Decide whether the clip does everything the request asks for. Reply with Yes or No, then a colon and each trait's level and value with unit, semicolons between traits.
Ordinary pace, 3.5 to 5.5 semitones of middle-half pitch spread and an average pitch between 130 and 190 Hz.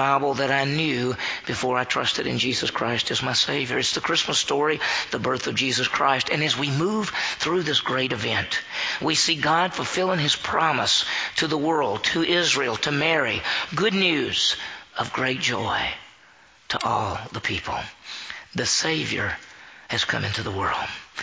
Yes: average, 165 wpm; average, 4.3 semitones; medium, 140 Hz